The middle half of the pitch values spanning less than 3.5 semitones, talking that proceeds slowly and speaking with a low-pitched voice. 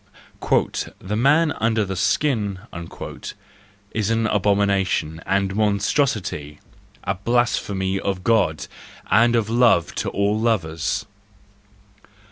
Yes: average, 3.0 semitones; slow, 95 wpm; low, 100 Hz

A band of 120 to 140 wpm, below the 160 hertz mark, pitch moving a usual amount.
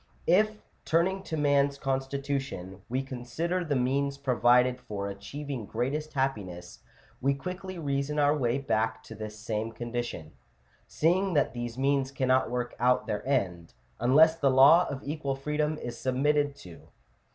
No: average, 150 wpm; low, 135 Hz; average, 3.5 semitones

